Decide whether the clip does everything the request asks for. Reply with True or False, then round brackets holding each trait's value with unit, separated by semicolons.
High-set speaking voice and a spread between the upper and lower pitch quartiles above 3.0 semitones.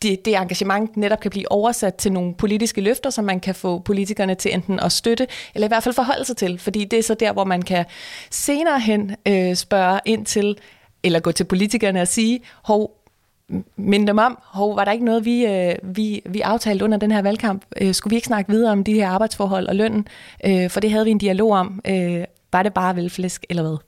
False (205 Hz; 2.5 semitones)